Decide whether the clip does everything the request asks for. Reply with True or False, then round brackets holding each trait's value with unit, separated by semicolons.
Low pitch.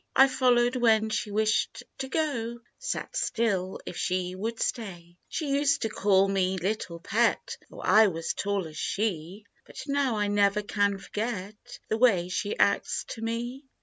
False (215 Hz)